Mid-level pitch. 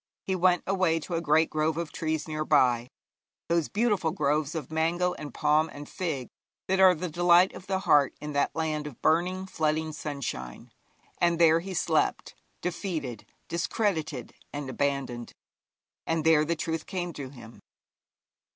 Yes: medium, 160 Hz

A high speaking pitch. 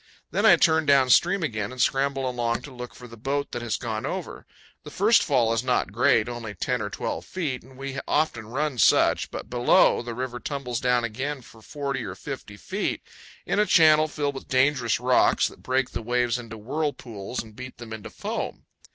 No: low, 125 Hz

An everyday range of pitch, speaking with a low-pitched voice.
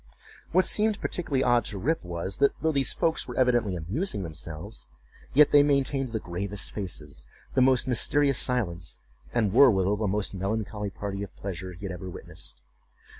No: wide, 6.2 semitones; low, 105 Hz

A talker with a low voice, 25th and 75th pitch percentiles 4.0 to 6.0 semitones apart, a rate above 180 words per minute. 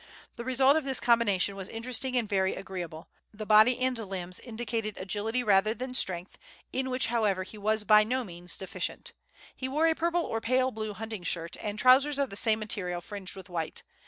No: high, 215 Hz; average, 4.7 semitones; average, 195 wpm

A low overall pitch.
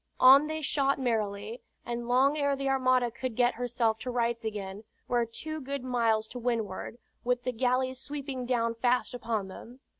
No: high, 245 Hz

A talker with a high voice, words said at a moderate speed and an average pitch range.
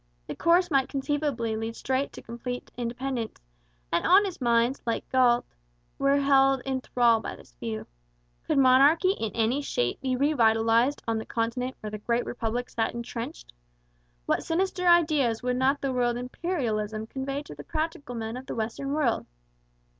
Yes: very high, 250 Hz; average, 165 wpm; average, 3.4 semitones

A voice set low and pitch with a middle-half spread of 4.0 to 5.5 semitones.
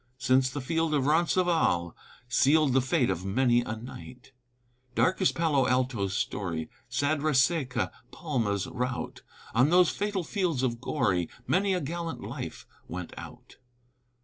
Yes: low, 130 Hz; average, 5.2 semitones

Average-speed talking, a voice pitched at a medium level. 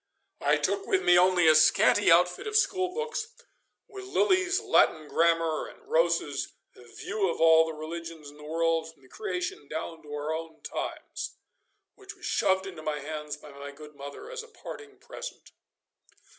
Yes: average, 170 wpm; medium, 165 Hz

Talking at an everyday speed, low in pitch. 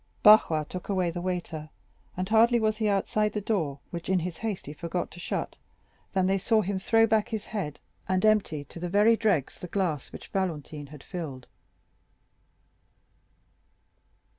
No: average, 165 wpm; medium, 185 Hz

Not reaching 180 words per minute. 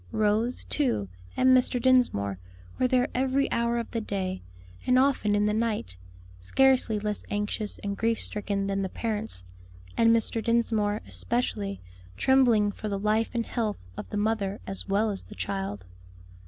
Yes: average, 160 wpm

